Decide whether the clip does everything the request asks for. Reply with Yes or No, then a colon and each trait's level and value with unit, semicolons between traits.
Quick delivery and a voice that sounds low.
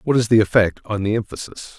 Yes: fast, 235 wpm; low, 105 Hz